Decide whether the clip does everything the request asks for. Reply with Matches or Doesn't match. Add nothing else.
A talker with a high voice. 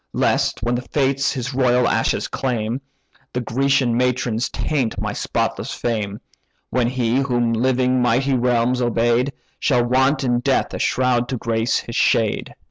Doesn't match